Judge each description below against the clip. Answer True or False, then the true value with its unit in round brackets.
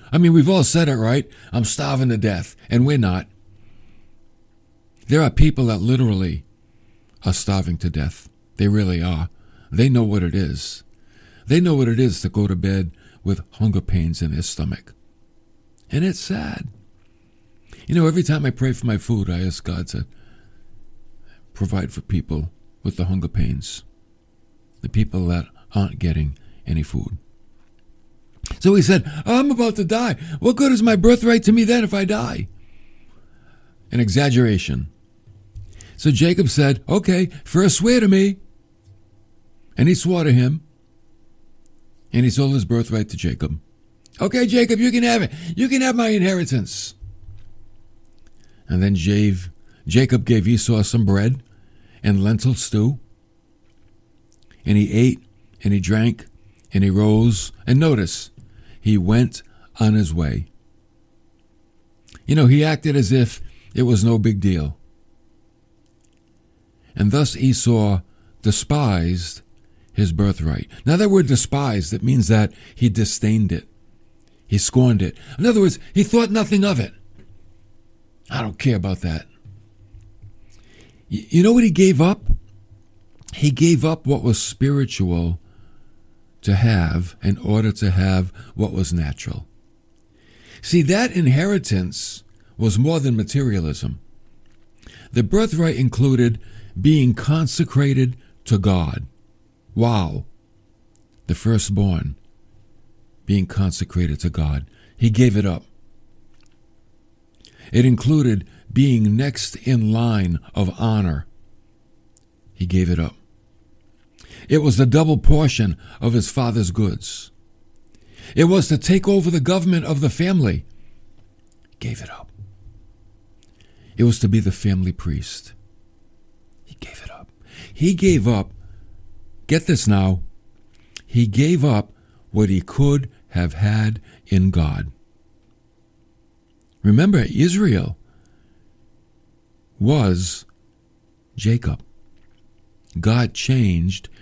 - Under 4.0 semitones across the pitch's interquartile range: False (4.6 semitones)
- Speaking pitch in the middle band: False (110 Hz)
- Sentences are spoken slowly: True (130 wpm)